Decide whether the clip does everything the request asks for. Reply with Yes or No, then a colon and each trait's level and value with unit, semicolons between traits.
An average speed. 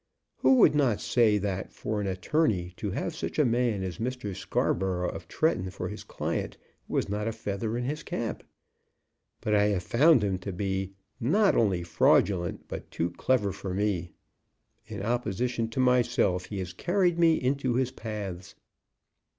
Yes: average, 165 wpm